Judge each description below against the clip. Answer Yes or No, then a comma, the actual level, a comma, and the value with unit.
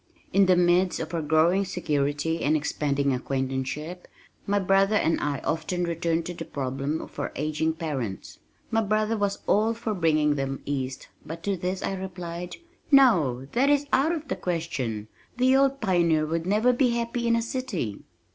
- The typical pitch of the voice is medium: Yes, medium, 170 Hz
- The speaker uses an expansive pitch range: Yes, wide, 5.7 semitones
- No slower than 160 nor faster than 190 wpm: Yes, average, 175 wpm